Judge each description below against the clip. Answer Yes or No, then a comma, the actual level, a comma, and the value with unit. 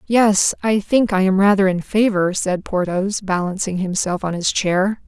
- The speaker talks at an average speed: Yes, average, 175 wpm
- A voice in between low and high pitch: No, high, 195 Hz